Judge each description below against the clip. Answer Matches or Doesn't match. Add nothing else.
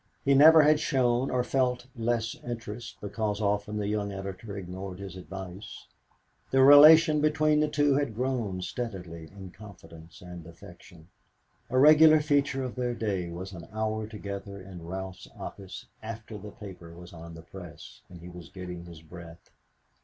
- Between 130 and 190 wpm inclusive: Matches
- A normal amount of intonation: Doesn't match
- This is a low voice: Matches